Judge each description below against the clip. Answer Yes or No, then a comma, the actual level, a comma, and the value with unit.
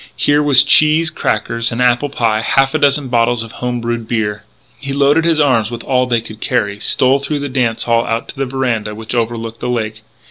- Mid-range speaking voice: No, low, 120 Hz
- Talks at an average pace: No, fast, 215 wpm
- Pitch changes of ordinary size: Yes, average, 3.4 semitones